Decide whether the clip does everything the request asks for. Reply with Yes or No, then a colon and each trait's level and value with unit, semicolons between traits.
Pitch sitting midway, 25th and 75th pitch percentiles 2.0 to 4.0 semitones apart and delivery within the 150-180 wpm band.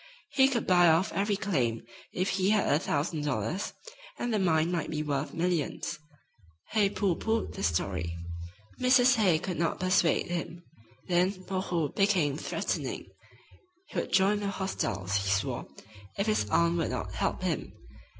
No: medium, 175 Hz; average, 4.6 semitones; average, 160 wpm